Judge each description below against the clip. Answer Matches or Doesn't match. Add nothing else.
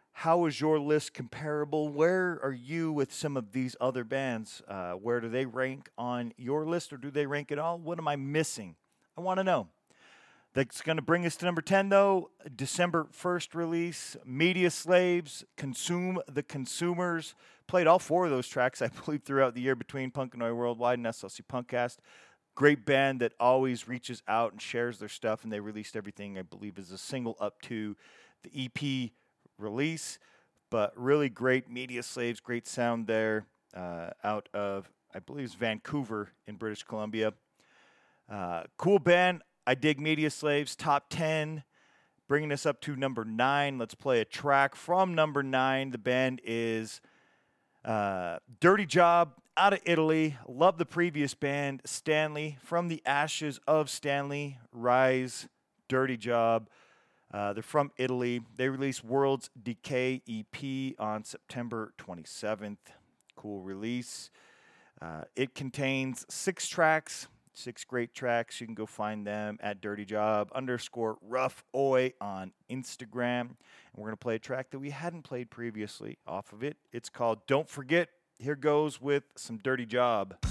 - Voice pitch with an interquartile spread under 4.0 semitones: Doesn't match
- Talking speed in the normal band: Matches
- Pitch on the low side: Matches